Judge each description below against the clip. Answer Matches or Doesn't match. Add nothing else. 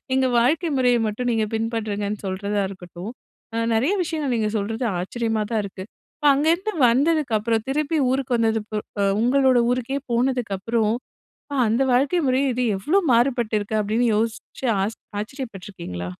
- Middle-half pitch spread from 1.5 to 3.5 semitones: Doesn't match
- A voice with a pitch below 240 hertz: Matches